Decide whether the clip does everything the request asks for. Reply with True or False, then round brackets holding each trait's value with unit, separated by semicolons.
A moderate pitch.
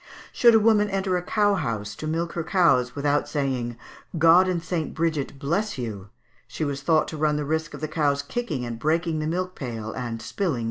True (155 Hz)